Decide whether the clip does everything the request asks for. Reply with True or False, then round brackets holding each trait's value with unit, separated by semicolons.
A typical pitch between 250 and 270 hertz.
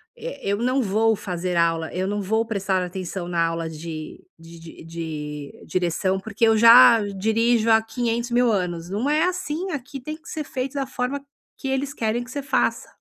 False (220 Hz)